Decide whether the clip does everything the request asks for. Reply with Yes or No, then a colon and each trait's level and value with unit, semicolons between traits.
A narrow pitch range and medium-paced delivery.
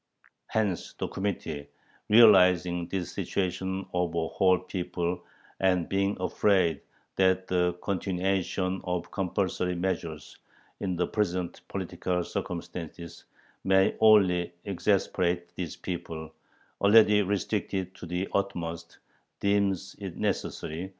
No: narrow, 1.9 semitones; slow, 105 wpm